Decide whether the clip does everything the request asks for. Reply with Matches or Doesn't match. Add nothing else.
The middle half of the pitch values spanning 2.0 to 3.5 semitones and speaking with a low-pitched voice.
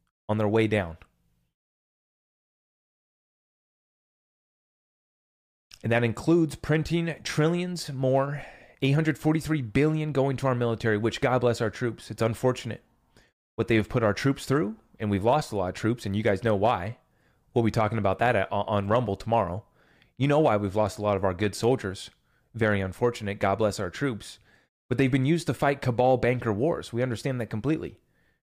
Doesn't match